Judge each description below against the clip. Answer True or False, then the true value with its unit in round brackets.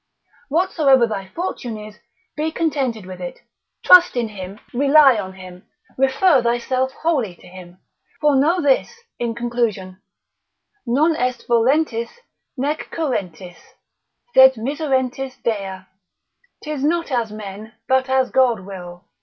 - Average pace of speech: False (125 wpm)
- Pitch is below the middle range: False (245 Hz)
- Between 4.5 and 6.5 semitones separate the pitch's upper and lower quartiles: True (5.3 semitones)